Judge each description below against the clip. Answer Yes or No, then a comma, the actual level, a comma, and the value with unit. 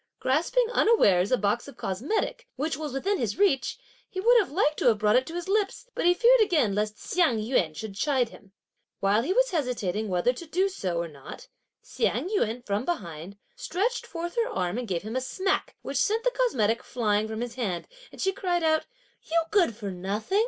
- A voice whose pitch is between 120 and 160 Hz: No, very high, 260 Hz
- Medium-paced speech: No, fast, 210 wpm